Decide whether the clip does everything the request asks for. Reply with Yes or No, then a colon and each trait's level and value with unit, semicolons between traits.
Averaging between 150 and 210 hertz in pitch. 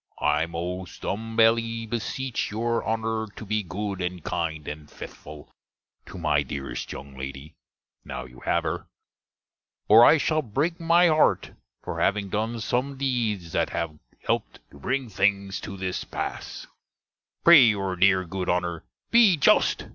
No: low, 100 Hz